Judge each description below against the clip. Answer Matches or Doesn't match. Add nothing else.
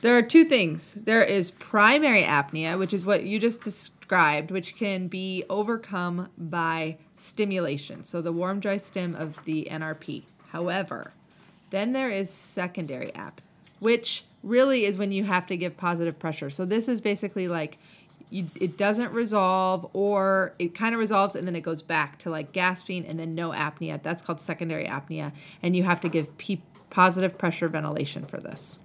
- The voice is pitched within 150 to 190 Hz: Matches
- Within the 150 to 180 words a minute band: Matches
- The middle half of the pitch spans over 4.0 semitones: Doesn't match